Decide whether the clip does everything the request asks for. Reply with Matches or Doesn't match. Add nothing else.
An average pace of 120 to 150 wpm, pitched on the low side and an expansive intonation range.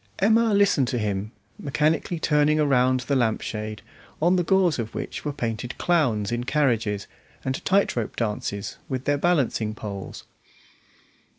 Matches